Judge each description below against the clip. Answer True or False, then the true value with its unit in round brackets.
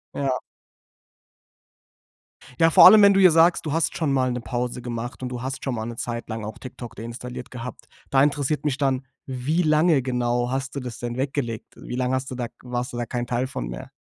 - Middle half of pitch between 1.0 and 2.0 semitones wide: False (2.5 semitones)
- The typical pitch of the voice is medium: False (125 Hz)